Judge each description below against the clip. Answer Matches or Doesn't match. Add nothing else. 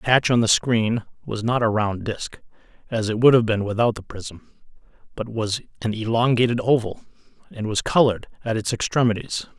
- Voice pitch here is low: Matches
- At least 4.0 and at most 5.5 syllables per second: Matches